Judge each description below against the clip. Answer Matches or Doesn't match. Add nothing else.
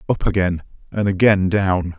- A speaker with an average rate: Matches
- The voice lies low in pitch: Matches